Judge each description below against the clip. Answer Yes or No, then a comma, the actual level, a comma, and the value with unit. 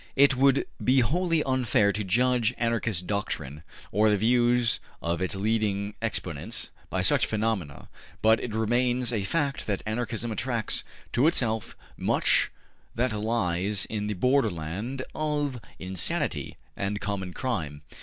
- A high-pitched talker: No, low, 110 Hz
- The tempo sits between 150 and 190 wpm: No, slow, 135 wpm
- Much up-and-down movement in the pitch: No, average, 4.0 semitones